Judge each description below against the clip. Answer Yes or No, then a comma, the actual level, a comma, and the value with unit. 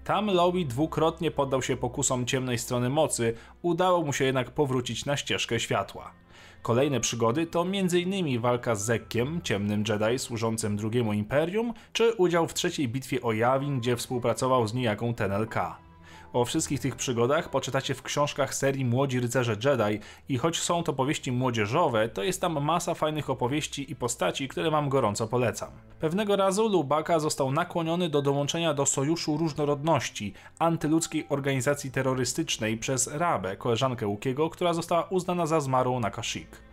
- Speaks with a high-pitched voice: No, low, 135 Hz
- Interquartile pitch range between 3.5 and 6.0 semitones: Yes, wide, 5.4 semitones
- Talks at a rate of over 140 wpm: Yes, average, 155 wpm